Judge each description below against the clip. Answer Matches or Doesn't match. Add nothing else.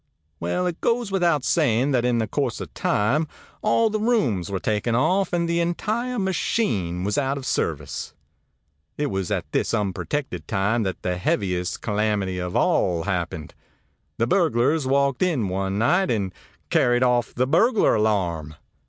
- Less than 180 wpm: Matches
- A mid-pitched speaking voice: Doesn't match